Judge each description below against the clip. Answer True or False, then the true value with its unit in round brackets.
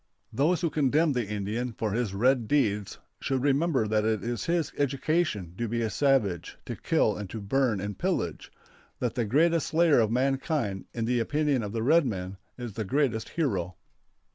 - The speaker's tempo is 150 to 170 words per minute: False (185 wpm)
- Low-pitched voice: True (120 Hz)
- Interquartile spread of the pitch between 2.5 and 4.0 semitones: False (5.2 semitones)